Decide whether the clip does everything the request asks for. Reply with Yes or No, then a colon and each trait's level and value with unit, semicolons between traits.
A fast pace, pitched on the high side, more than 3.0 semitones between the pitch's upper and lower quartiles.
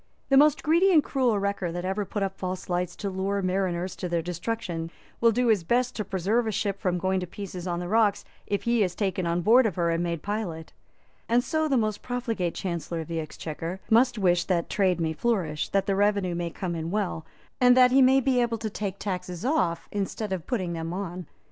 Yes: fast, 225 wpm; high, 195 Hz; average, 4.5 semitones